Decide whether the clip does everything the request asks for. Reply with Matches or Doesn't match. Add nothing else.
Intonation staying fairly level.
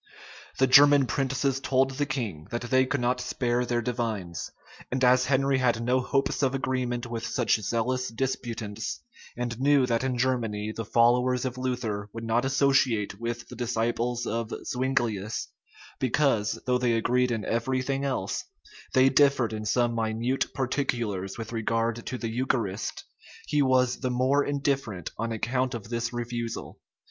Matches